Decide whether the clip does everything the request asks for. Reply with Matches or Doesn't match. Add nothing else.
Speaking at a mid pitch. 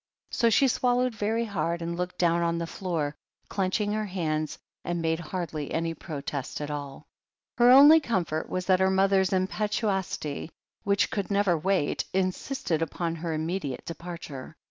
Matches